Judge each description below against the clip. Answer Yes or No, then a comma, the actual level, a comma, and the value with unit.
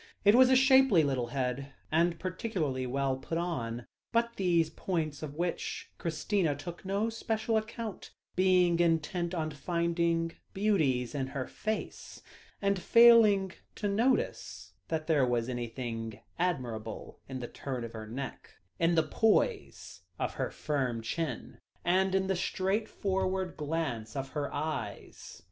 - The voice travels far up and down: Yes, wide, 6.3 semitones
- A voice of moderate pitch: Yes, medium, 165 Hz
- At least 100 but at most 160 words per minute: Yes, average, 140 wpm